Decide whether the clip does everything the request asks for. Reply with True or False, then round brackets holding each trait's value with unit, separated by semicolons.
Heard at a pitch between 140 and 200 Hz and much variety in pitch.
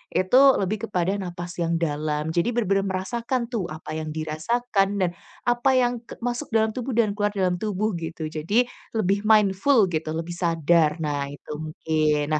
True (185 Hz; 5.7 semitones)